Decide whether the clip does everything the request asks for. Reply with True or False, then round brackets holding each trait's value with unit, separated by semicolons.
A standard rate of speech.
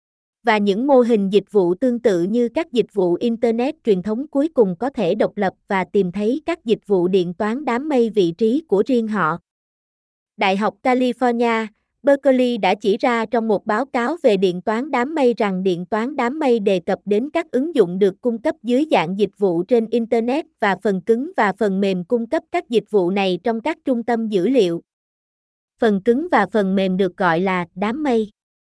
True (210 wpm)